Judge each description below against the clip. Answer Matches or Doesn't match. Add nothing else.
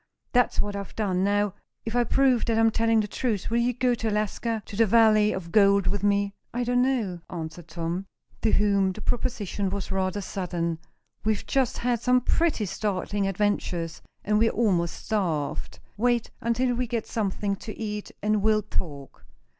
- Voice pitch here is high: Matches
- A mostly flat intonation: Doesn't match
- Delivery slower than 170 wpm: Doesn't match